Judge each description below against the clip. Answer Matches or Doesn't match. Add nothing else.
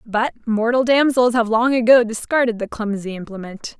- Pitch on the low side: Doesn't match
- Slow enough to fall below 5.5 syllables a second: Matches